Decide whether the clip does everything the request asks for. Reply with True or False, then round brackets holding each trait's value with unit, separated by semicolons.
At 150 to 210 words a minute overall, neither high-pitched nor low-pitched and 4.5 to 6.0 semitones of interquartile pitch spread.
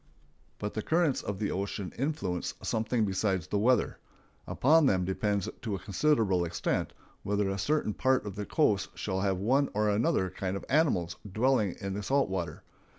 False (175 wpm; 105 Hz; 5.2 semitones)